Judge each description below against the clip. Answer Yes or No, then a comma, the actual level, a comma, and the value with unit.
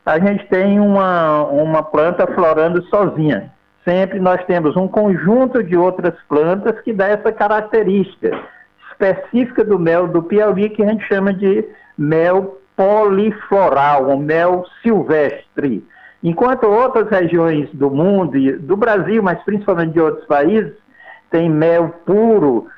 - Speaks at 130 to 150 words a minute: Yes, average, 135 wpm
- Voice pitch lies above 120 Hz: Yes, high, 190 Hz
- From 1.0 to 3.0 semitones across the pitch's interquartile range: No, average, 4.0 semitones